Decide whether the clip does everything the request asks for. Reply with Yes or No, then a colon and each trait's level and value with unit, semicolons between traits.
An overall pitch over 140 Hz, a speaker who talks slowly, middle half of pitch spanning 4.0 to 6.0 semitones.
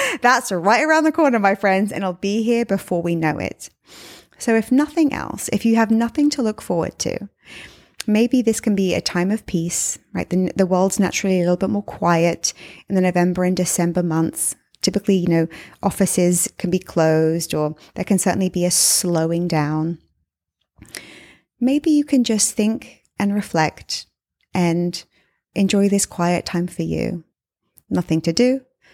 No: high, 190 Hz; average, 170 wpm; average, 4.4 semitones